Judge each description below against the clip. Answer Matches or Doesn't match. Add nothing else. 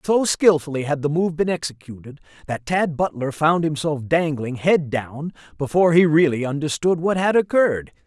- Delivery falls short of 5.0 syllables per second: Doesn't match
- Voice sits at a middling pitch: Matches